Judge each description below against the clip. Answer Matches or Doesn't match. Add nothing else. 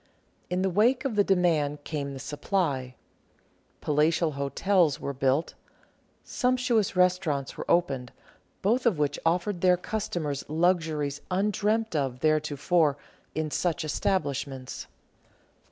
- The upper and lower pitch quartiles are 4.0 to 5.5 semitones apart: Matches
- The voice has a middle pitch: Matches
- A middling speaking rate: Doesn't match